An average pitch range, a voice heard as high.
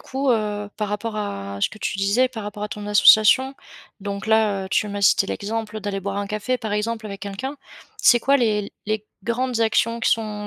No: narrow, 2.0 semitones; high, 210 Hz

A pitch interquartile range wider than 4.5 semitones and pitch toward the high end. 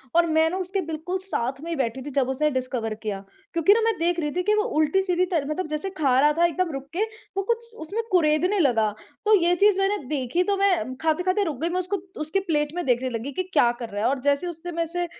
Yes: average, 5.0 semitones; very high, 325 Hz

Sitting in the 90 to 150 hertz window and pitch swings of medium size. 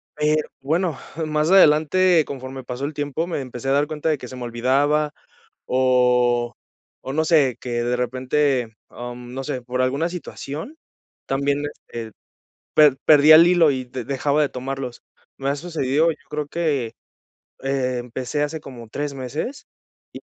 Yes: medium, 140 Hz; average, 3.2 semitones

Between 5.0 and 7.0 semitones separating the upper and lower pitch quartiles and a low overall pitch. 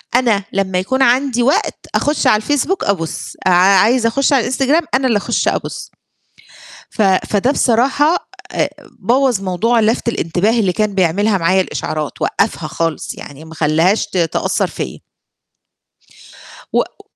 No: wide, 5.6 semitones; high, 215 Hz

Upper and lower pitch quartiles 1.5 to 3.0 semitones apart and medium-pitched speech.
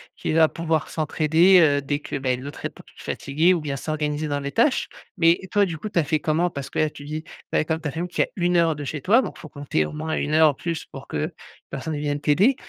Yes: narrow, 2.5 semitones; medium, 155 Hz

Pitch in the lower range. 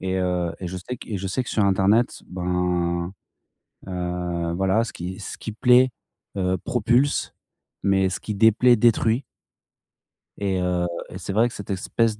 Yes: very low, 95 Hz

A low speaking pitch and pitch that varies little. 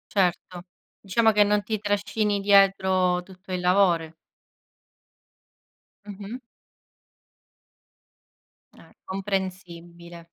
No: high, 190 Hz; narrow, 2.3 semitones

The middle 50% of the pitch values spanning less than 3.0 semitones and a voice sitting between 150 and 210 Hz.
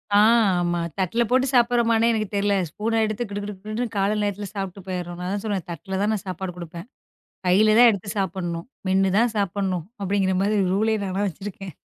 Yes: narrow, 2.6 semitones; high, 200 Hz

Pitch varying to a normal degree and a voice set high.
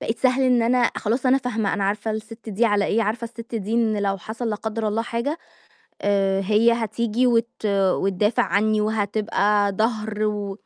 No: narrow, 2.1 semitones; high, 220 Hz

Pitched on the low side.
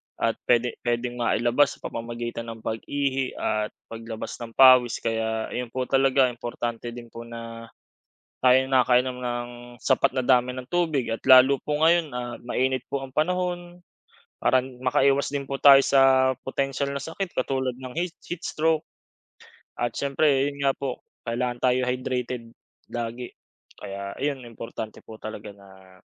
Yes: low, 125 Hz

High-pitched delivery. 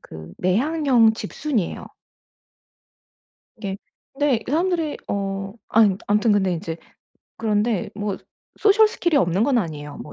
Yes: high, 215 Hz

